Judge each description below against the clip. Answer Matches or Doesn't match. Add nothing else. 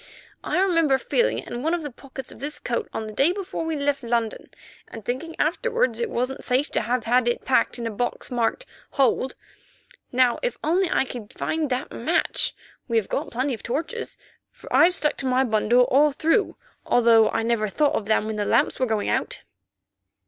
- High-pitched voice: Matches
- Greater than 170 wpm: Matches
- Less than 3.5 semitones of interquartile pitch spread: Doesn't match